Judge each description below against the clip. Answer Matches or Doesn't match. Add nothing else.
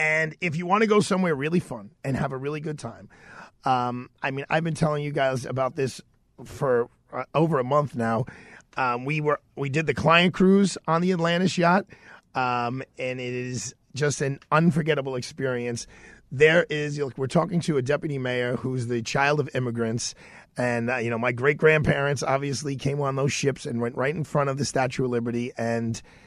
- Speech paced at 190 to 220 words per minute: Matches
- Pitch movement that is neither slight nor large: Matches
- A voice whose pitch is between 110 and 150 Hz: Matches